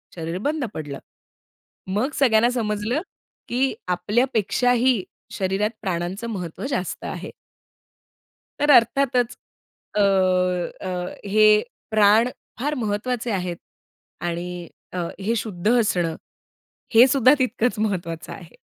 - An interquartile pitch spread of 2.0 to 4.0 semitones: No, average, 5.1 semitones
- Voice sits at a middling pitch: No, high, 210 Hz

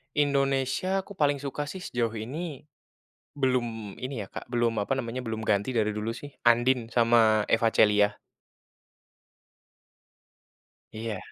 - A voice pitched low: Yes, low, 120 Hz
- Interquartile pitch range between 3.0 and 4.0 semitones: Yes, average, 3.7 semitones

